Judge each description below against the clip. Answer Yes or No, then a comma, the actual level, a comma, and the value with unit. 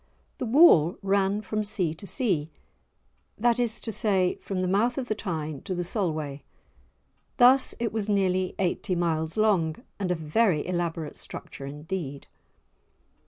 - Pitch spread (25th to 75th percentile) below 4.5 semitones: No, average, 5.1 semitones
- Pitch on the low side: No, medium, 185 Hz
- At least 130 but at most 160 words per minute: Yes, average, 150 wpm